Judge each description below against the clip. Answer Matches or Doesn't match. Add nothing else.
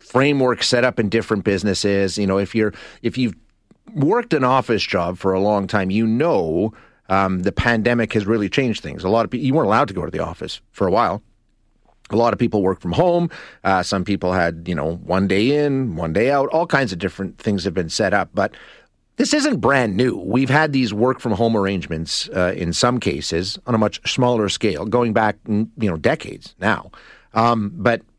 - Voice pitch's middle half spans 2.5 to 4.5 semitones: Matches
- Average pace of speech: Doesn't match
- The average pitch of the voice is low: Matches